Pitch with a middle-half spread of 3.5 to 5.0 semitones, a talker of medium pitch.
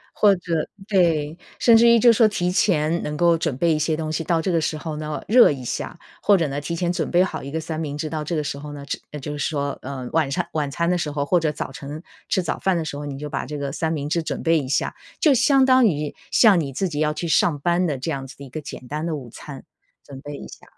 No: average, 3.1 semitones; medium, 155 Hz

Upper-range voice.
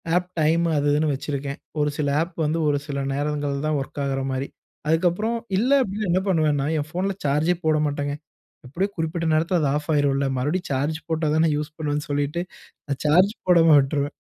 No: medium, 150 Hz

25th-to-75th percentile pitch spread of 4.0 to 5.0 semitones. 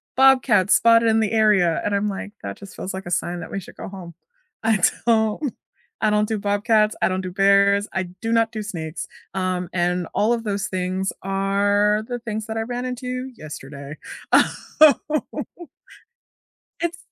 No: average, 3.2 semitones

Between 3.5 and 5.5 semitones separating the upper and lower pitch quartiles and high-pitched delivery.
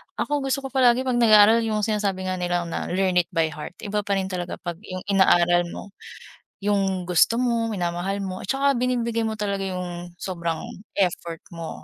Yes: average, 4.0 semitones; high, 195 Hz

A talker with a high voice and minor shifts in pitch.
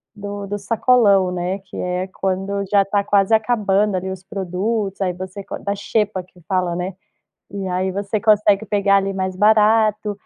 Yes: high, 200 Hz; narrow, 1.8 semitones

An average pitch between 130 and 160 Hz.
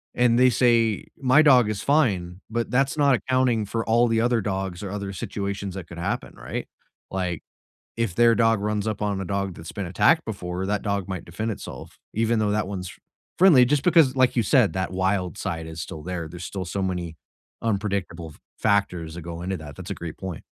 No: low, 100 Hz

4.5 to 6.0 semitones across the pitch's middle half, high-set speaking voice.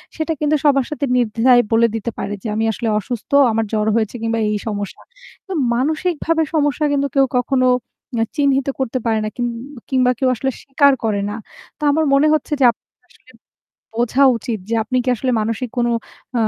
No: average, 3.9 semitones; very high, 255 Hz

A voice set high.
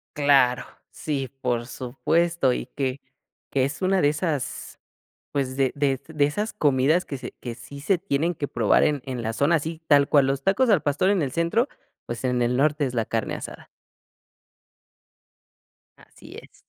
No: medium, 140 Hz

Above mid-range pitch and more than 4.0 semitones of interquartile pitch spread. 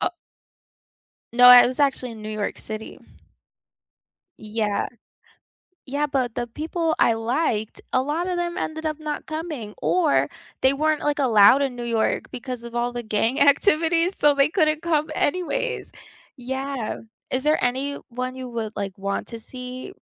Yes: very high, 260 Hz; average, 4.6 semitones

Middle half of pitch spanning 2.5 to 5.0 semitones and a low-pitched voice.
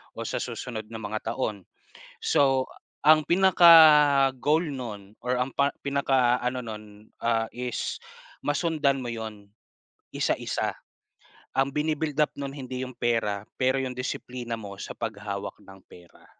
Yes: average, 4.2 semitones; low, 125 Hz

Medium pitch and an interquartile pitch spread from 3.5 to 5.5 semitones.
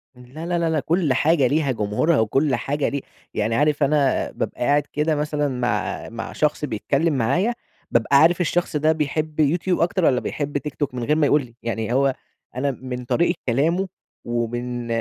Yes: medium, 145 Hz; average, 4.0 semitones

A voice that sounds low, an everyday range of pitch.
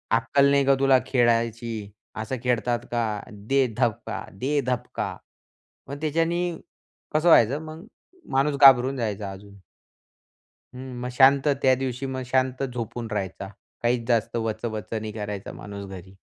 Yes: low, 120 Hz; average, 3.8 semitones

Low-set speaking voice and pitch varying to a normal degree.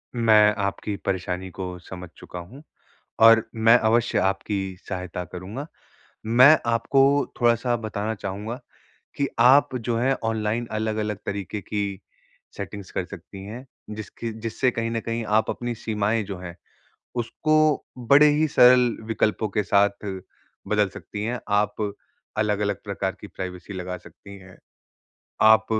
Yes: low, 110 Hz; average, 3.0 semitones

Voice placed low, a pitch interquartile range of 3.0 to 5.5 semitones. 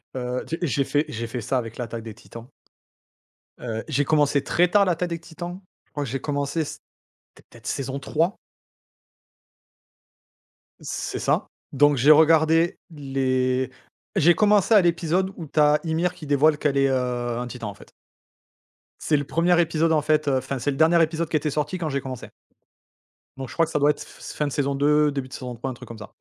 No: medium, 145 Hz; average, 3.8 semitones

